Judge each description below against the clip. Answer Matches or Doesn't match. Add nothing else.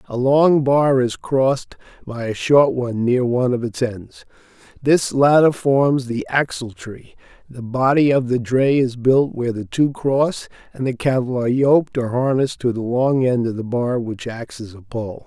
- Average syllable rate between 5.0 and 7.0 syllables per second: Doesn't match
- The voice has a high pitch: Doesn't match